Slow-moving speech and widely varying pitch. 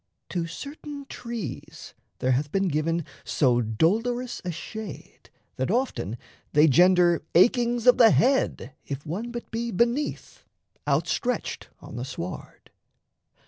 Yes: slow, 125 wpm; wide, 8.2 semitones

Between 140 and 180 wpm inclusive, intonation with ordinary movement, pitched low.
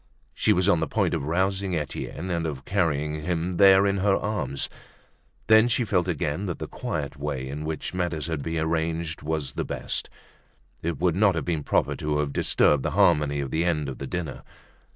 No: average, 200 wpm; average, 3.5 semitones; very low, 80 Hz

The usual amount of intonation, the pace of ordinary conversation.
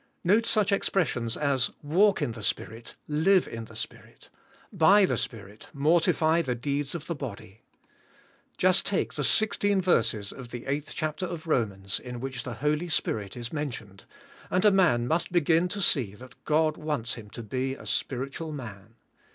No: wide, 6.6 semitones; average, 175 wpm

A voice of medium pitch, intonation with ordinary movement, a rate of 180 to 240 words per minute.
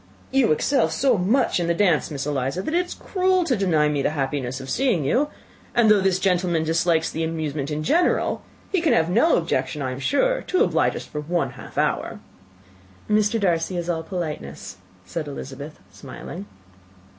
No: medium, 170 Hz; wide, 6.8 semitones; average, 185 wpm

